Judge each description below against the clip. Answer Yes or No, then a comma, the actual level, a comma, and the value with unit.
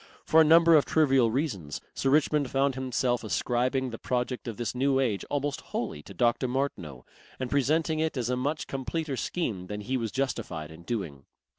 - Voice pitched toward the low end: Yes, low, 130 Hz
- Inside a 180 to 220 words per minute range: Yes, average, 185 wpm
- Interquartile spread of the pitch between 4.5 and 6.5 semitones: No, average, 3.7 semitones